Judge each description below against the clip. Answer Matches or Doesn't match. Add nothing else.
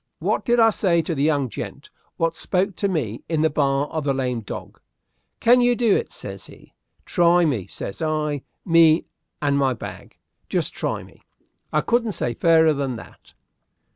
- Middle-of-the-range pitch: Matches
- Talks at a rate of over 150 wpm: Matches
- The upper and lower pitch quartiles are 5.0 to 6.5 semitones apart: Doesn't match